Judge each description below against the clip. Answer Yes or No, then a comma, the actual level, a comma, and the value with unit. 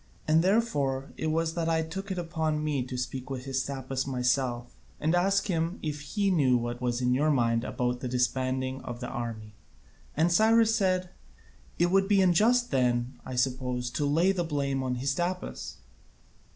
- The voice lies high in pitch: No, medium, 140 Hz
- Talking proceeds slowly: No, average, 175 wpm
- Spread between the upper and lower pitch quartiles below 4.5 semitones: No, wide, 5.6 semitones